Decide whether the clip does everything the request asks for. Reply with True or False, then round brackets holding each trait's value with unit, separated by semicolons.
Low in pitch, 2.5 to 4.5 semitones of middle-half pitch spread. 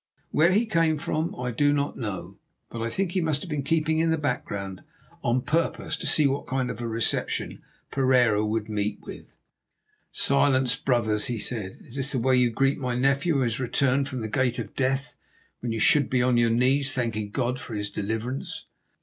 True (130 Hz; 3.6 semitones)